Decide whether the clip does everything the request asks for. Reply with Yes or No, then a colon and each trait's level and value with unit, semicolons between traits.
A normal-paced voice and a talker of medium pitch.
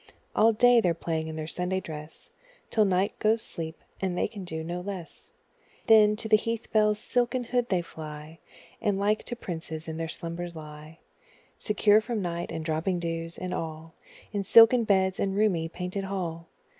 Yes: average, 180 wpm; medium, 180 Hz